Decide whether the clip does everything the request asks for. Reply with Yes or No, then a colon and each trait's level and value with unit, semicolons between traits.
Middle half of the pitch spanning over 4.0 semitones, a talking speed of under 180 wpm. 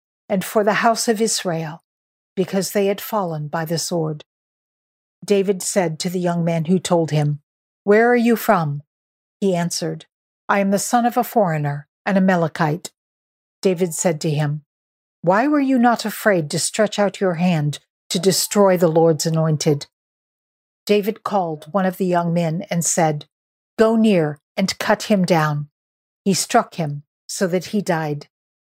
Yes: average, 4.4 semitones; average, 165 wpm